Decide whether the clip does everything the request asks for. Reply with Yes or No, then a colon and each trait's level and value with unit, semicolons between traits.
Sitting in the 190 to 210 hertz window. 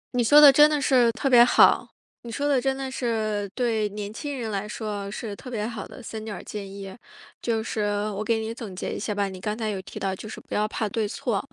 No: high, 220 Hz